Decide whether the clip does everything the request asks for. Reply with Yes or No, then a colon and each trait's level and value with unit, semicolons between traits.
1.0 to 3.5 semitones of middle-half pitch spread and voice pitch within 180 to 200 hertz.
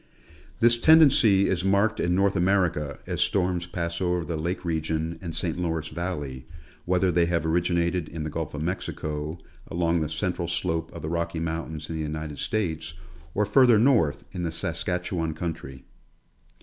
No: narrow, 2.4 semitones; very low, 85 Hz